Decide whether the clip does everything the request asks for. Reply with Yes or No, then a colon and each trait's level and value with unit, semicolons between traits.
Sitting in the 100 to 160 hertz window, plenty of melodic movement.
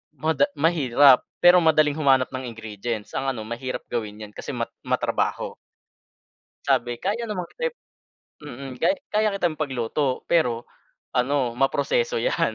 Yes: low, 135 Hz; wide, 5.8 semitones